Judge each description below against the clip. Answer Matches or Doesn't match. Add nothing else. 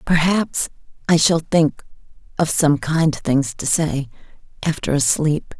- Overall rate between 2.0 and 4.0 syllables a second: Matches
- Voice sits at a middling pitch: Matches